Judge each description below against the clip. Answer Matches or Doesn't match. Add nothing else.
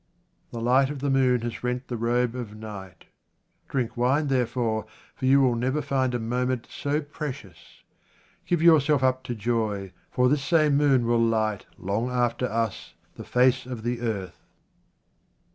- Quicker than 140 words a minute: Matches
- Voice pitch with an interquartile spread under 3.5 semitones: Matches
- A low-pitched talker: Matches